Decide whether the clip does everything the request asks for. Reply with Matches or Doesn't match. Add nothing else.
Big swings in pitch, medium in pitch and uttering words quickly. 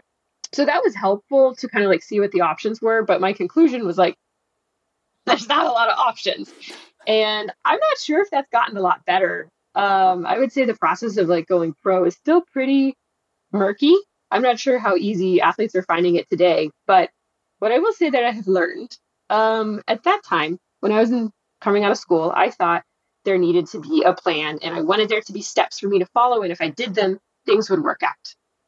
Doesn't match